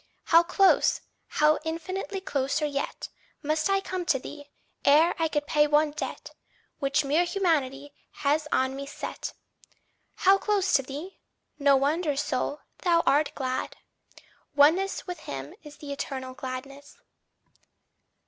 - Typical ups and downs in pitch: Yes, average, 3.4 semitones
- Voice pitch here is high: Yes, very high, 295 Hz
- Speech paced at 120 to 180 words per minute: Yes, slow, 135 wpm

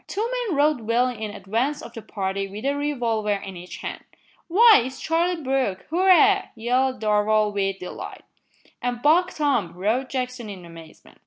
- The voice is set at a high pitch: Yes, high, 240 Hz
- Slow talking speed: No, average, 165 wpm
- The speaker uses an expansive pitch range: Yes, wide, 5.9 semitones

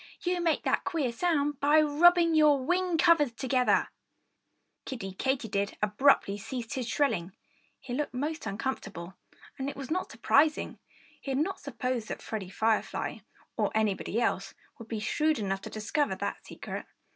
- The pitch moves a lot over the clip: Yes, wide, 5.7 semitones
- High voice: Yes, very high, 265 Hz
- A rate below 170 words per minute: Yes, average, 155 wpm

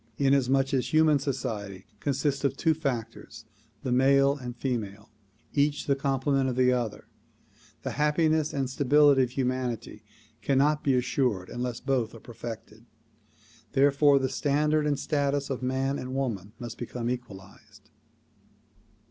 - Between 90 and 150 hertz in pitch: Yes, low, 135 Hz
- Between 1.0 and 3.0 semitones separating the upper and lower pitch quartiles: Yes, average, 2.7 semitones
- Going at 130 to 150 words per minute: Yes, average, 140 wpm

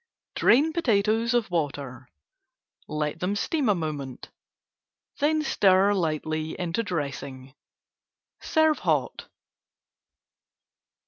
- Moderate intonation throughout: No, wide, 7.3 semitones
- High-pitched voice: No, medium, 180 Hz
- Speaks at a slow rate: Yes, slow, 85 wpm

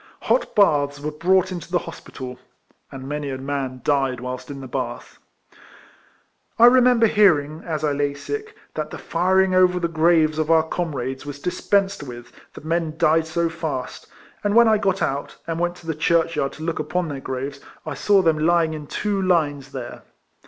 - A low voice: No, medium, 160 Hz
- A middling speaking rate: Yes, average, 190 wpm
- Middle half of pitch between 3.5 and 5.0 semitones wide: Yes, average, 4.0 semitones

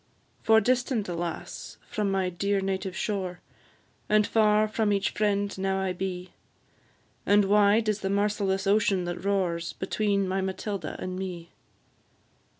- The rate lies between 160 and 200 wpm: No, average, 140 wpm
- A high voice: Yes, high, 195 Hz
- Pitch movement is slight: Yes, narrow, 1.8 semitones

